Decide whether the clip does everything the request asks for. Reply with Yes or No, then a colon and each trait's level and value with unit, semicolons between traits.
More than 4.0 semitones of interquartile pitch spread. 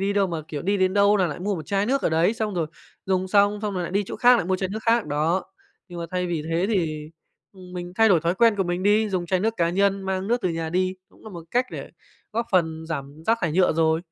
No: average, 3.3 semitones